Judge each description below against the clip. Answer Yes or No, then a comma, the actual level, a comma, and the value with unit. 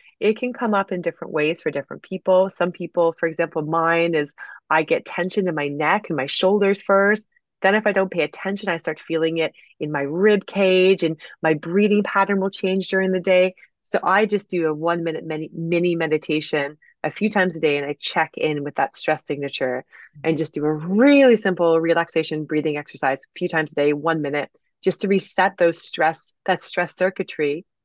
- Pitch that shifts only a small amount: No, average, 3.6 semitones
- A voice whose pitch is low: No, medium, 170 Hz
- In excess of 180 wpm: Yes, fast, 205 wpm